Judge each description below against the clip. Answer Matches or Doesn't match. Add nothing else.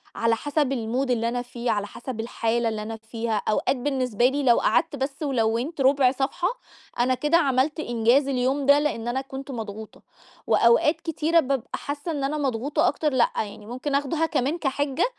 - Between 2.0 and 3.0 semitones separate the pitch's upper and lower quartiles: Doesn't match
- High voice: Matches